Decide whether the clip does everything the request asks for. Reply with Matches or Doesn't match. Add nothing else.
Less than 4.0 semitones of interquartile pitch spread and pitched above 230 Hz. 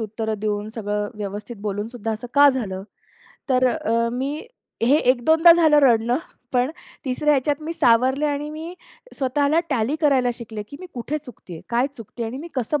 Doesn't match